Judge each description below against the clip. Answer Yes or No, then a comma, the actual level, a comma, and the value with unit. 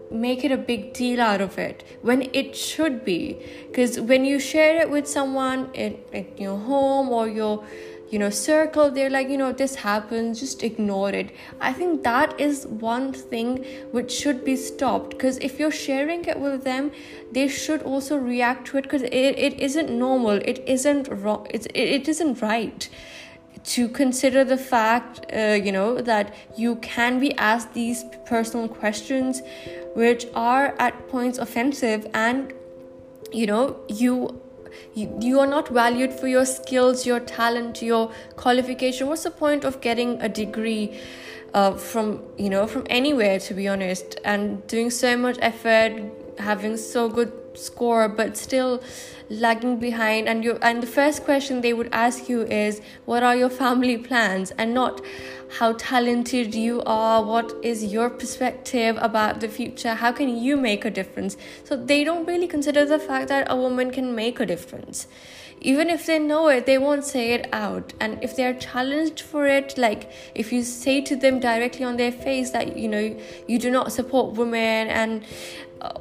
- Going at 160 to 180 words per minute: Yes, average, 175 wpm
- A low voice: No, high, 245 Hz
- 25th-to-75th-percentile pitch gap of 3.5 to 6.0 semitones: No, average, 2.9 semitones